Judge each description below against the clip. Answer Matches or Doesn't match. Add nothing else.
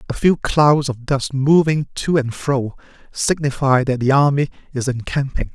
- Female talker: Doesn't match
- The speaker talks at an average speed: Matches